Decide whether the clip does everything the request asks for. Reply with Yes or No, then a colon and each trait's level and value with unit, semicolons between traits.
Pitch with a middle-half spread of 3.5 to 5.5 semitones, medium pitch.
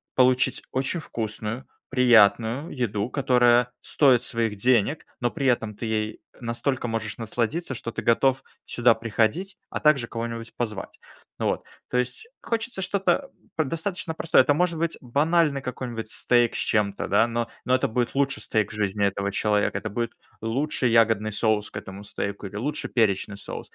No: average, 3.8 semitones; low, 120 Hz